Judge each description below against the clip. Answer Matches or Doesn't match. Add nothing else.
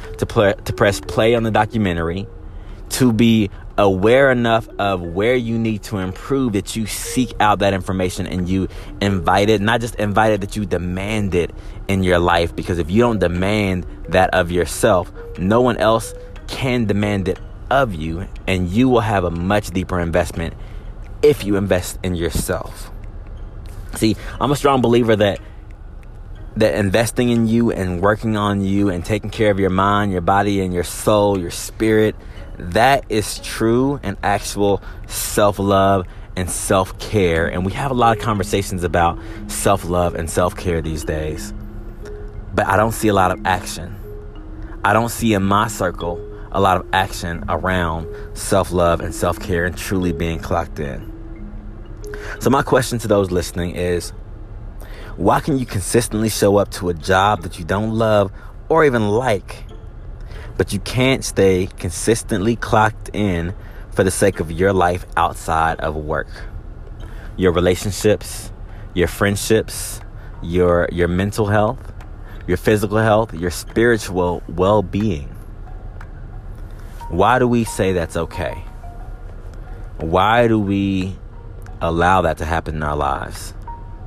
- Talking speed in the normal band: Matches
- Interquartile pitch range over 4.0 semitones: Doesn't match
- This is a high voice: Doesn't match